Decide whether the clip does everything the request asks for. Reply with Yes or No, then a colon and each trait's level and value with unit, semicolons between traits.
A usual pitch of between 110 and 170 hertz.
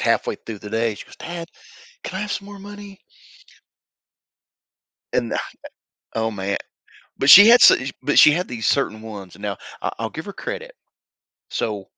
Yes: medium, 140 Hz